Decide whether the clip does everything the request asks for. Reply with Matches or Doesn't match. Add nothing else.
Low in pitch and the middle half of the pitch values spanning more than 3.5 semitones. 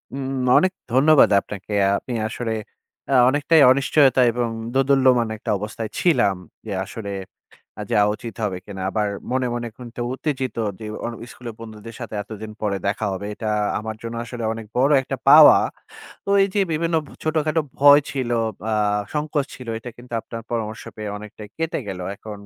Matches